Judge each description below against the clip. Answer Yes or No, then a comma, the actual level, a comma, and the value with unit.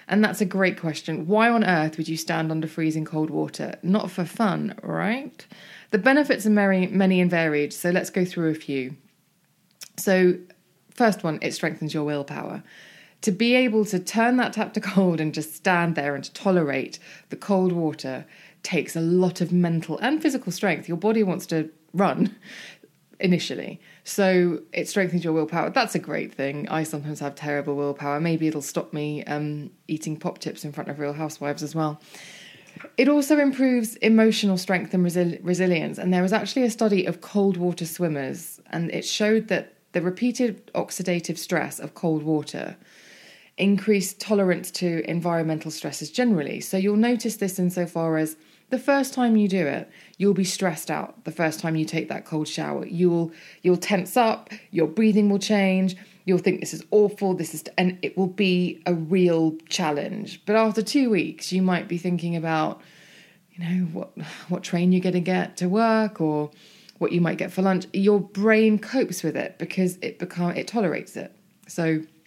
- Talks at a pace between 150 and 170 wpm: No, average, 180 wpm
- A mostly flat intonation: No, average, 4.0 semitones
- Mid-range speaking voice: Yes, medium, 180 Hz